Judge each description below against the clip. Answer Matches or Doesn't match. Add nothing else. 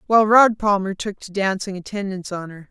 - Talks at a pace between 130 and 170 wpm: Doesn't match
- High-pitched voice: Matches